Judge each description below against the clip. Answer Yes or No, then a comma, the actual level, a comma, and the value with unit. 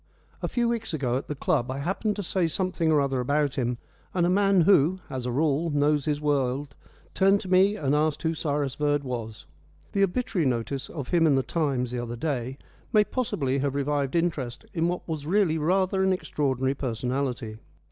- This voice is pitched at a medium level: Yes, medium, 145 Hz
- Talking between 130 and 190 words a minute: No, average, 200 wpm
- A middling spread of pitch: Yes, average, 4.9 semitones